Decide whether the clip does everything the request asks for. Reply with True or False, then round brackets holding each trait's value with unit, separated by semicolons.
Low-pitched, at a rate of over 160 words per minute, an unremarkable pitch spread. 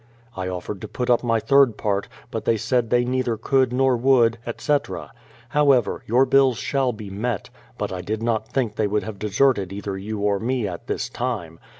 True (115 Hz; 200 wpm; 3.8 semitones)